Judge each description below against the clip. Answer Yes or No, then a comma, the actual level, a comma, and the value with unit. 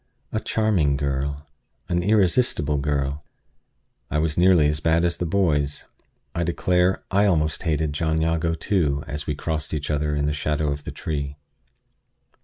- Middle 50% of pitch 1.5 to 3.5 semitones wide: Yes, average, 2.9 semitones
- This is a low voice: Yes, very low, 75 Hz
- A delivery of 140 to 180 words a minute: Yes, average, 160 wpm